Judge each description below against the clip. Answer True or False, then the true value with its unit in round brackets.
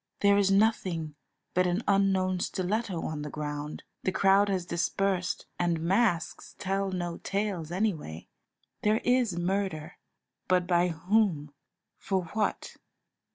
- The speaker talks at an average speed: False (125 wpm)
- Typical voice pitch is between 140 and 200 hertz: True (185 Hz)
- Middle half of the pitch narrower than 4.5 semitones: True (2.8 semitones)